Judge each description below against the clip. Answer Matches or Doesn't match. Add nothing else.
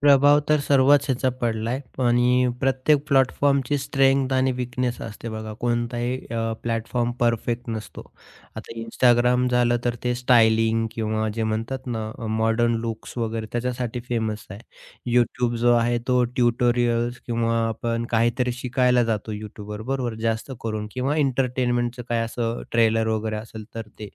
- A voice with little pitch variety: Matches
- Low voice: Matches